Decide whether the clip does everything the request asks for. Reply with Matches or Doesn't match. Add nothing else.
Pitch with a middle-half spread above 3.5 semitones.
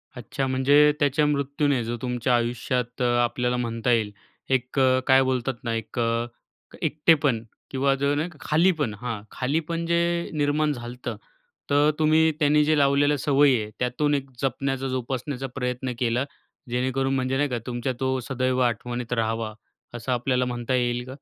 Doesn't match